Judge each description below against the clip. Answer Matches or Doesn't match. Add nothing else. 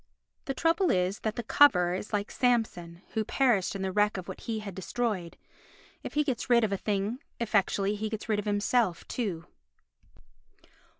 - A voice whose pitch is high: Matches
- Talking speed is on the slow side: Doesn't match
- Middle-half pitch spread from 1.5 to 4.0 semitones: Matches